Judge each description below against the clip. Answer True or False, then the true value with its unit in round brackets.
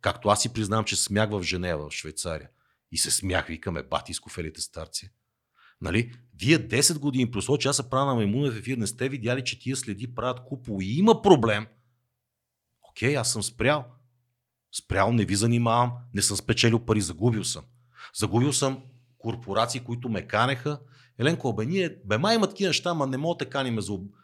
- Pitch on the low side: True (120 Hz)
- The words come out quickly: True (185 wpm)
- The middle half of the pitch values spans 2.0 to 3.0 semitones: False (4.2 semitones)